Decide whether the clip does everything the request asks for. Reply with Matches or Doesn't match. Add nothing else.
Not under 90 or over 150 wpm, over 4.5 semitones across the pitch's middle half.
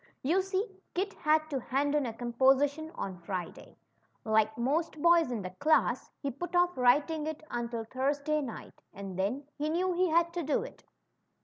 Doesn't match